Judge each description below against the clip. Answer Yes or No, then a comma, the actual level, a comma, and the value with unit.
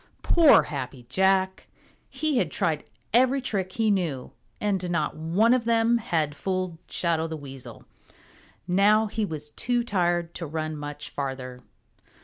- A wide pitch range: Yes, wide, 6.1 semitones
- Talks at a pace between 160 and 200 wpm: No, average, 140 wpm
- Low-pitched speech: No, medium, 180 Hz